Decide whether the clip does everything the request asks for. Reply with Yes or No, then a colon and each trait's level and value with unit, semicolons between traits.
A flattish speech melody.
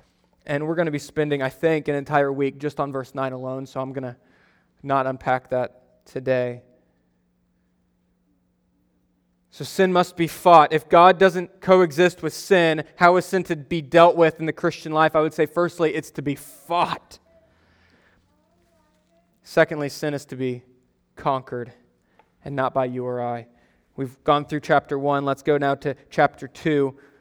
No: average, 4.0 semitones